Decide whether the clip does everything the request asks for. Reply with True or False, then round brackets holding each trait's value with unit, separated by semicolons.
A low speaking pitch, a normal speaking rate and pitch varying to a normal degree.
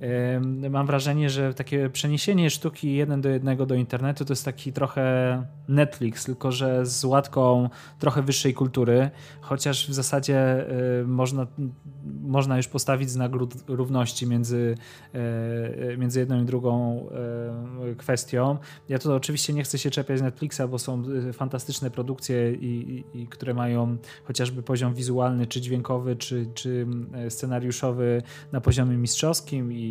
False (130 Hz; 130 wpm; 2.0 semitones)